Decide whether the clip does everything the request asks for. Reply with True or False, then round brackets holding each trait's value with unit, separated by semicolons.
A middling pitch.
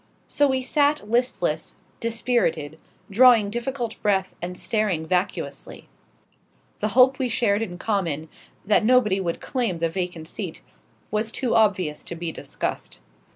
False (210 Hz)